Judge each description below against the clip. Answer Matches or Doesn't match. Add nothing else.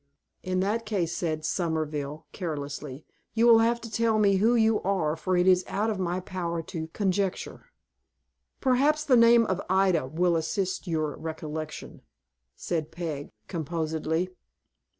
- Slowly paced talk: Doesn't match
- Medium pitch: Matches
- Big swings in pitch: Doesn't match